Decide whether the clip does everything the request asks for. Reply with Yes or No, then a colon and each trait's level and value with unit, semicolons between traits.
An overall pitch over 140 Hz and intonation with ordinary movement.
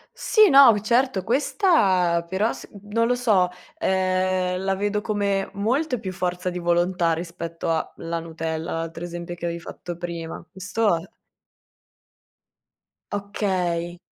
Yes: medium, 185 Hz; average, 3.3 semitones